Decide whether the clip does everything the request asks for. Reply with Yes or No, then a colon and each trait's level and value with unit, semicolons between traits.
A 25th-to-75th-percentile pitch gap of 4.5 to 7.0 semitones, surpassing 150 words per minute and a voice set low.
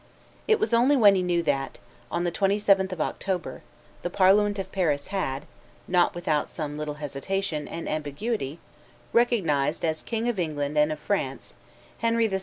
No: average, 5.2 semitones; average, 165 wpm; medium, 175 Hz